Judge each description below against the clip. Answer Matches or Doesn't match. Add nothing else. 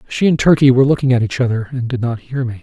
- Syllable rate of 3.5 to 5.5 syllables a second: Doesn't match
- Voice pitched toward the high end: Doesn't match